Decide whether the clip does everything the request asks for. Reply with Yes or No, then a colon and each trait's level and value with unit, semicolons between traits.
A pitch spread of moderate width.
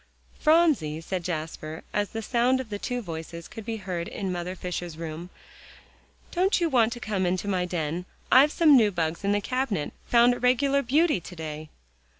No: wide, 6.6 semitones